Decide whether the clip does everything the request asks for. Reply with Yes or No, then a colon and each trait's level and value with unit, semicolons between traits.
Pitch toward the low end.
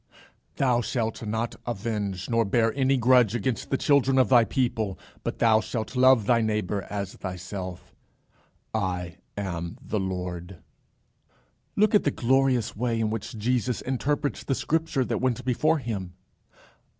Yes: low, 115 Hz